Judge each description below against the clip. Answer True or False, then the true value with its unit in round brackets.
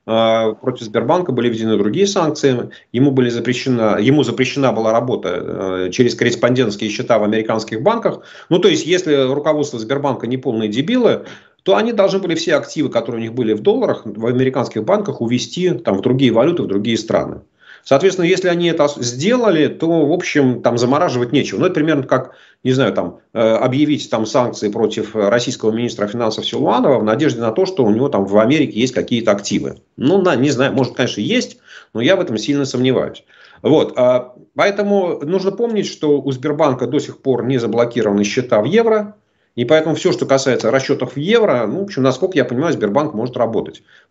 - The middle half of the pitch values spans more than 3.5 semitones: True (4.9 semitones)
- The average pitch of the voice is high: False (130 Hz)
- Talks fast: True (180 wpm)